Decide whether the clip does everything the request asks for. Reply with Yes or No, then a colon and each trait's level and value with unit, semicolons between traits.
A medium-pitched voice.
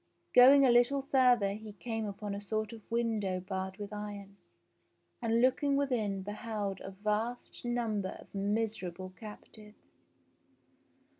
No: high, 215 Hz